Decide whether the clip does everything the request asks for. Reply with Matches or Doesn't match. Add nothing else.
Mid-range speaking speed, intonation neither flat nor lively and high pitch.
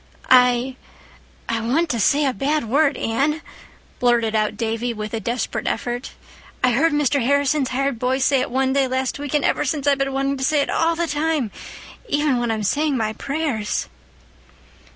Matches